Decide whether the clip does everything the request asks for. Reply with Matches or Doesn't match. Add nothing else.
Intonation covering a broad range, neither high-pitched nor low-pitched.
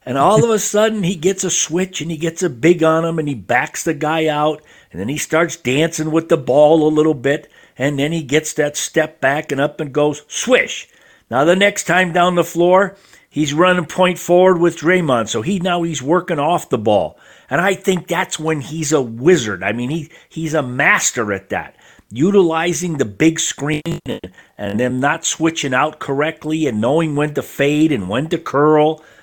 Doesn't match